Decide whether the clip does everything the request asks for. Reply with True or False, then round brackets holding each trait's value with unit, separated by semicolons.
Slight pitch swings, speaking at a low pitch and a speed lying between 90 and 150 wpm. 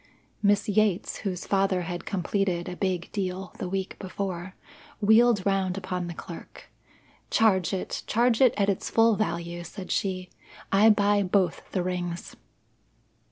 False (2.2 semitones; 190 Hz; 145 wpm)